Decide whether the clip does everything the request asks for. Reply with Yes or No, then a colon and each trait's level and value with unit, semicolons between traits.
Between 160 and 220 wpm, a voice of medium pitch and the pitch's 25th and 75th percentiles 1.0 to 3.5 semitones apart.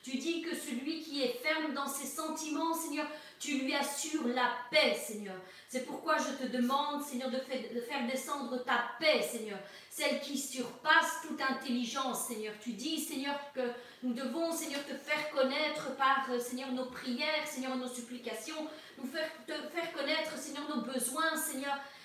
No: average, 165 wpm; very high, 275 Hz; average, 3.2 semitones